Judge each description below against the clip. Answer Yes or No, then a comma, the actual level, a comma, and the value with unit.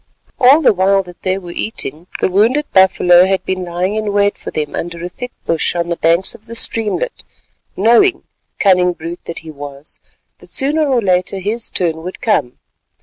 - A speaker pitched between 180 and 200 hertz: Yes, medium, 185 Hz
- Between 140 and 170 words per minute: No, average, 180 wpm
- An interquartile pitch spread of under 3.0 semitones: No, average, 4.0 semitones